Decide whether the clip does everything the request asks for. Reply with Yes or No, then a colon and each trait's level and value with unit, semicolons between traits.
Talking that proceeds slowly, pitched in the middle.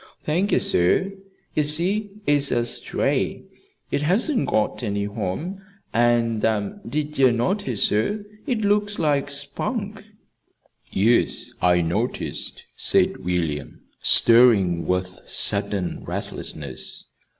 No: slow, 105 wpm; low, 125 Hz